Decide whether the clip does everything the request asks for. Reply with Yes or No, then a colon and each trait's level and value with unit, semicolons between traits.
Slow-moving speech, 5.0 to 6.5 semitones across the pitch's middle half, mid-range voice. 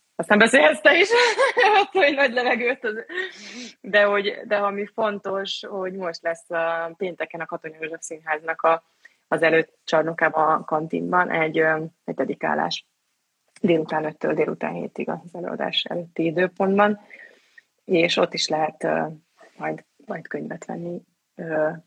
No: average, 125 wpm; wide, 5.5 semitones; medium, 175 Hz